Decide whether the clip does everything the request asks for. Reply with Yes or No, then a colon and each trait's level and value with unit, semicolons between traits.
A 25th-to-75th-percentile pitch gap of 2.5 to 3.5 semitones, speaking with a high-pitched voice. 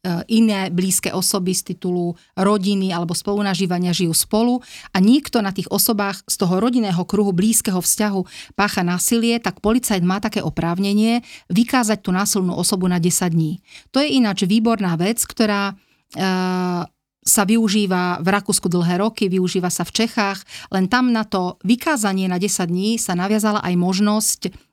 Yes: average, 2.9 semitones; high, 195 Hz